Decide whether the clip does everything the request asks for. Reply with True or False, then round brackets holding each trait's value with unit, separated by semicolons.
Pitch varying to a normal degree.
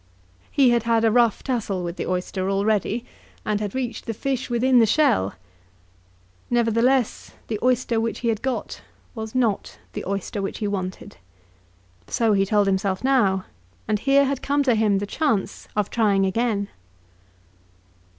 True (3.7 semitones)